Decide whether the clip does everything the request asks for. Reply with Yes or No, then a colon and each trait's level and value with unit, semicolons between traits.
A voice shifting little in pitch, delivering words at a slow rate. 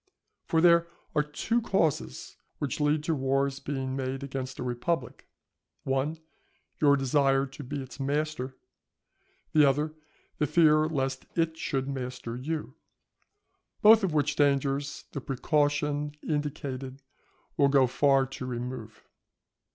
Yes: narrow, 2.2 semitones; slow, 130 wpm